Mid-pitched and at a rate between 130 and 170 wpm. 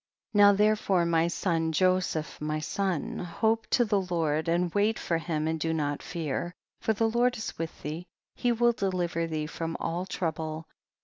No: medium, 170 Hz; average, 180 wpm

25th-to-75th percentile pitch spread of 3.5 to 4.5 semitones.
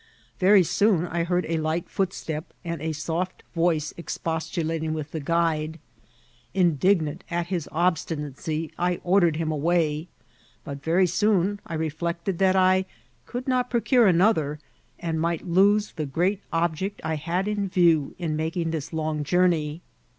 No: average, 2.7 semitones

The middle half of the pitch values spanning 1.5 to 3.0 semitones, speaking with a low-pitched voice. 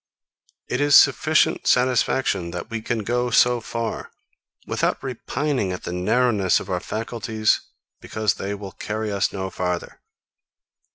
No: average, 4.2 semitones; low, 110 Hz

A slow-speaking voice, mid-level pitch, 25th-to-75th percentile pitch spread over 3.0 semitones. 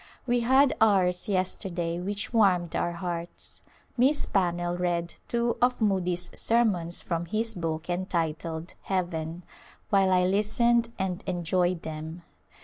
Yes: slow, 130 wpm; medium, 180 Hz; average, 3.5 semitones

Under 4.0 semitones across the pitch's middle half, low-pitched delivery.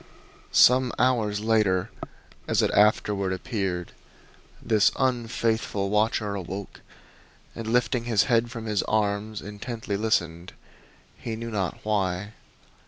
Yes: narrow, 2.5 semitones; low, 105 Hz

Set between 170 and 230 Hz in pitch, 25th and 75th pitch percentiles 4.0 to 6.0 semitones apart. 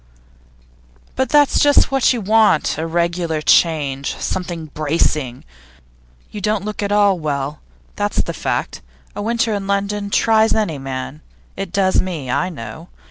Yes: medium, 185 Hz; average, 5.3 semitones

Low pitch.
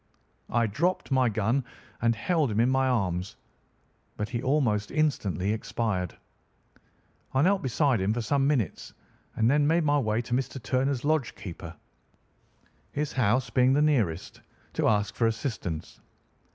Yes: low, 120 Hz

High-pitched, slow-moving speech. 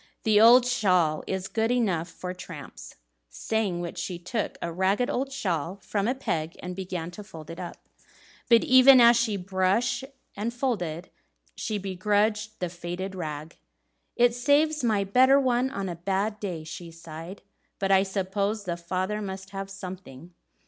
No: high, 195 Hz; average, 165 wpm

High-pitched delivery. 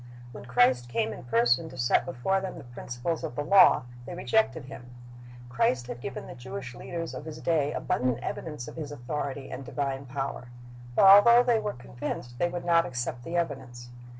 No: low, 135 Hz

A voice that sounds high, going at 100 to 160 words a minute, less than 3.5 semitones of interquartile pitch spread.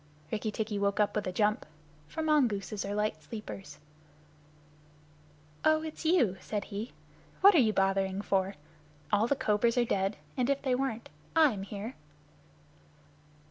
No: high, 215 Hz; average, 150 wpm; average, 4.2 semitones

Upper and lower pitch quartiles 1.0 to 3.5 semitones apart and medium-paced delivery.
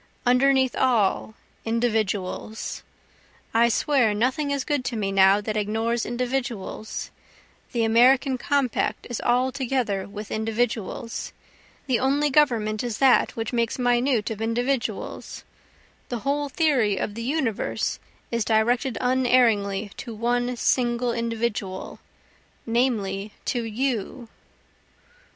No: average, 2.9 semitones; slow, 110 wpm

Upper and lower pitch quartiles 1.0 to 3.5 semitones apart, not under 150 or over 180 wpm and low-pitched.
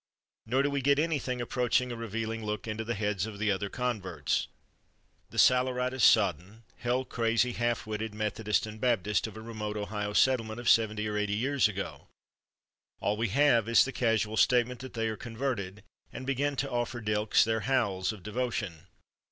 Yes: average, 2.9 semitones; average, 175 wpm; low, 115 Hz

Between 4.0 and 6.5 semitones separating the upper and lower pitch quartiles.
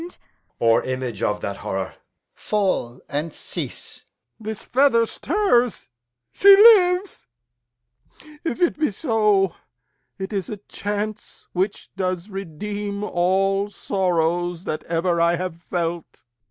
Yes: average, 4.4 semitones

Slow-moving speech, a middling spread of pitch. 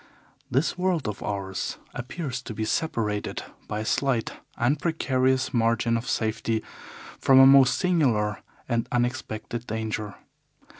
Yes: slow, 130 wpm; average, 3.5 semitones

